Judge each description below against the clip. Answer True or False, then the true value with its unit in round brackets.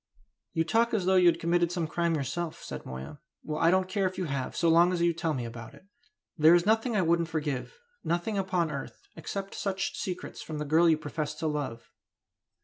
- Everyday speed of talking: False (225 wpm)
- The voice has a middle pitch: True (170 Hz)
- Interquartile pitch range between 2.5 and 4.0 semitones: True (3.4 semitones)